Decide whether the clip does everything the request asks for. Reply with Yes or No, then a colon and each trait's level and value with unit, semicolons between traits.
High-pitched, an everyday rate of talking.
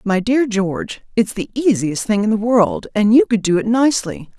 No: high, 220 Hz; fast, 220 wpm